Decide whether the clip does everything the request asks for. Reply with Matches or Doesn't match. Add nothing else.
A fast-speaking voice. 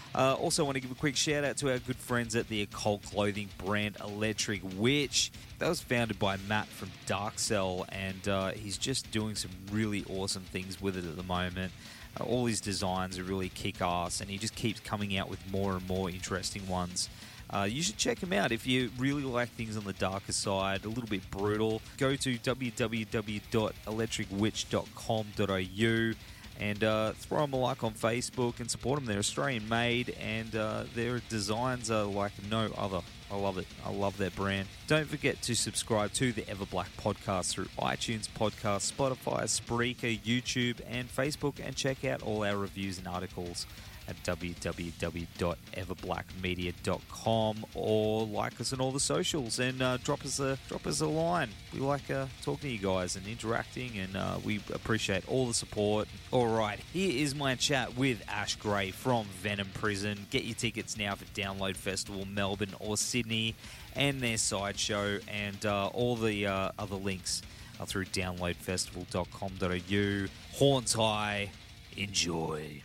Doesn't match